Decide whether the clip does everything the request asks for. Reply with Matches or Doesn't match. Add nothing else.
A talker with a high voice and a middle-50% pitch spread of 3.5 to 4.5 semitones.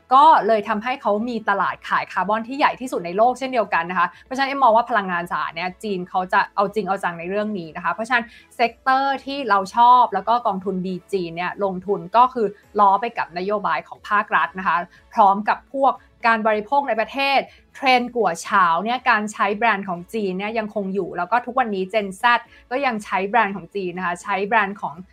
Matches